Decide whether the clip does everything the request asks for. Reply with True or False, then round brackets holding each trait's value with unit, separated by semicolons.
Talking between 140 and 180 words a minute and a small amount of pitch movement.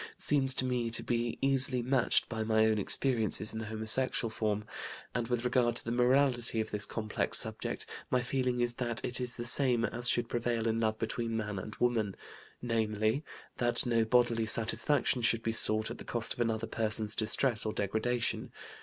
False (190 wpm; 1.9 semitones)